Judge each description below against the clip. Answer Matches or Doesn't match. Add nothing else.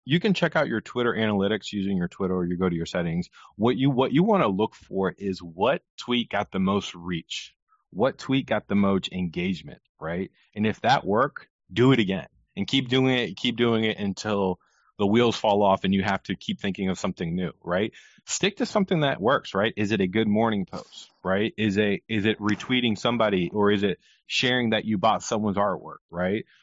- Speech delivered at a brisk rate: Matches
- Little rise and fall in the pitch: Doesn't match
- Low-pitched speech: Matches